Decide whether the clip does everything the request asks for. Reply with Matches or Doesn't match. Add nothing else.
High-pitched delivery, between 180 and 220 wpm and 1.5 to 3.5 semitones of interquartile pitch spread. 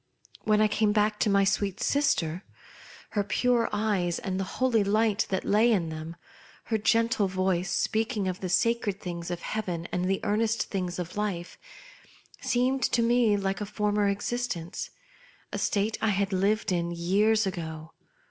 Doesn't match